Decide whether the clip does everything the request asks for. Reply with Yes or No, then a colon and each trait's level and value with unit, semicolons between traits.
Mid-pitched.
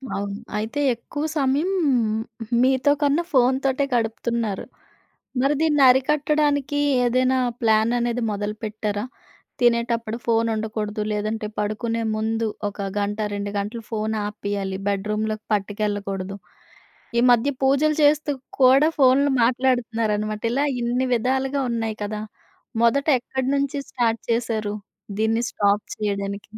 No: high, 230 Hz